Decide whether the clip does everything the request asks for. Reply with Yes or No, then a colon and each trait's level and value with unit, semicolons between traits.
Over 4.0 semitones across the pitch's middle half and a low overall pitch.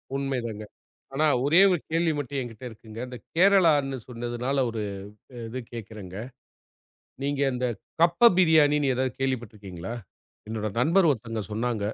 Yes: average, 4.4 semitones; low, 125 Hz